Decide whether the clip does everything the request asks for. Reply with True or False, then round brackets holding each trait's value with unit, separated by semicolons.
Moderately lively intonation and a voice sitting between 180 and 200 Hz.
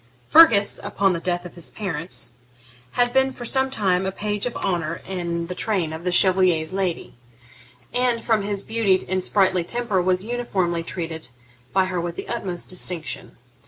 True (3.5 semitones; 185 Hz)